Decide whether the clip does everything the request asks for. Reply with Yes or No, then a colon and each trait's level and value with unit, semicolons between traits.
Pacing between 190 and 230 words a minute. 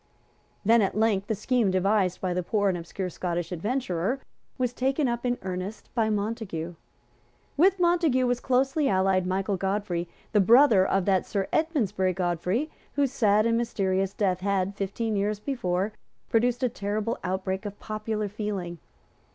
No: average, 155 wpm